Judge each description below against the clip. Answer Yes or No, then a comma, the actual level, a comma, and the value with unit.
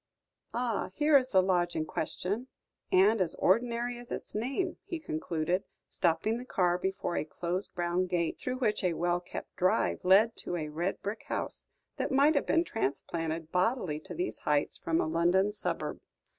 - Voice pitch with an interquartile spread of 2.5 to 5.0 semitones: No, wide, 5.6 semitones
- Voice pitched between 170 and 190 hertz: Yes, medium, 185 Hz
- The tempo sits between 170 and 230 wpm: Yes, average, 175 wpm